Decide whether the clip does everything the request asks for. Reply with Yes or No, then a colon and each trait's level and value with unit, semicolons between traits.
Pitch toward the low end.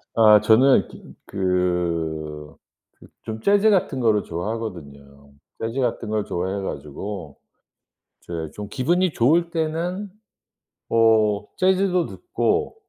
Yes: low, 110 Hz